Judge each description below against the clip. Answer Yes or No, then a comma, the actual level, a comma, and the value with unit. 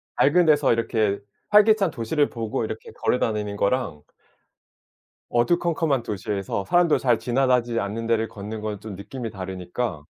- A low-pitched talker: Yes, low, 115 Hz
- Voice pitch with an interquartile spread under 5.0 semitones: Yes, average, 4.6 semitones